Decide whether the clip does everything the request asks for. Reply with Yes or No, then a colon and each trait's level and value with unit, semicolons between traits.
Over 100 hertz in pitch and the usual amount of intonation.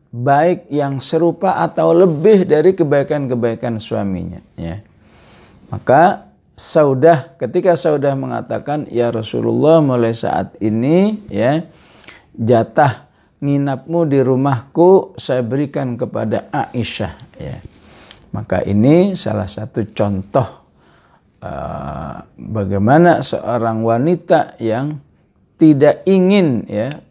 No: low, 135 Hz; wide, 6.3 semitones